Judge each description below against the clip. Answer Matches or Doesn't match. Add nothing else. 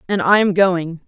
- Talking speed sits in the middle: Doesn't match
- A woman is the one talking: Matches